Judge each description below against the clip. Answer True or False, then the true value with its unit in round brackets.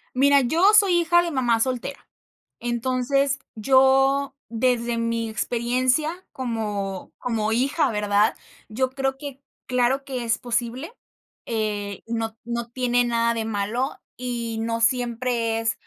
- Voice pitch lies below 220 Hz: False (240 Hz)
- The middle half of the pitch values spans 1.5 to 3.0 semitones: True (2.7 semitones)